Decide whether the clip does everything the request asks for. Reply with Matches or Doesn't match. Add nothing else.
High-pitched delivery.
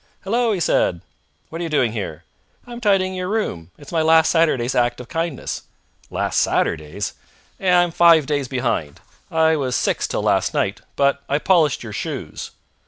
Doesn't match